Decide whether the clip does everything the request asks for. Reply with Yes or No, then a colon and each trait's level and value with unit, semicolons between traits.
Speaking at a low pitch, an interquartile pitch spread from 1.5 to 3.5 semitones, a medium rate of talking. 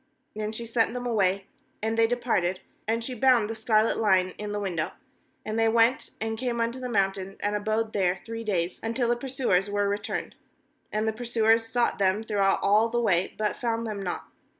No: high, 220 Hz; narrow, 2.5 semitones; average, 195 wpm